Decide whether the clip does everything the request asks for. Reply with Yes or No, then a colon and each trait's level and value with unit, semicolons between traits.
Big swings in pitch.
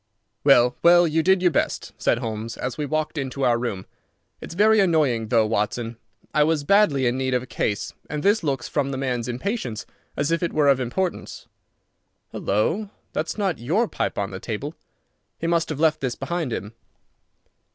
Yes: wide, 5.7 semitones